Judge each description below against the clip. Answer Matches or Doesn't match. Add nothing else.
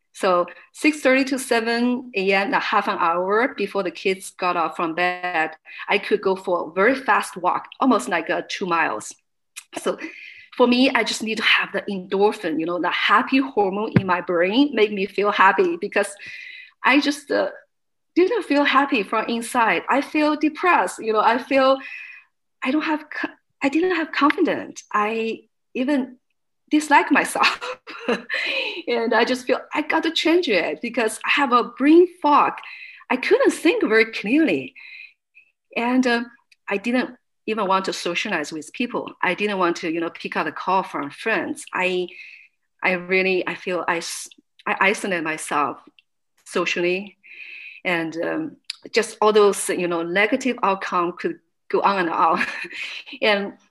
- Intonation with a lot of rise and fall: Matches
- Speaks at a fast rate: Doesn't match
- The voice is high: Matches